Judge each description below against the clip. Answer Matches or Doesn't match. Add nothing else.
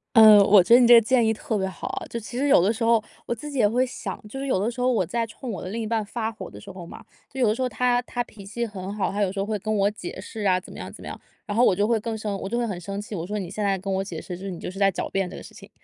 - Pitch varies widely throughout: Doesn't match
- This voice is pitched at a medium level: Doesn't match